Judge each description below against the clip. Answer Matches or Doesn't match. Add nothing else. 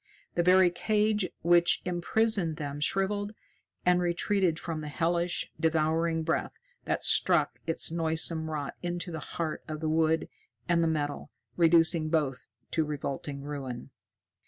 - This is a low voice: Doesn't match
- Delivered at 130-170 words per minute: Matches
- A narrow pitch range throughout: Matches